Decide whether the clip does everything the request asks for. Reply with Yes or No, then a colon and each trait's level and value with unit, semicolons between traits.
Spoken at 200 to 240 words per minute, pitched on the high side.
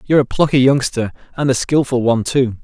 No: fast, 205 wpm; low, 130 Hz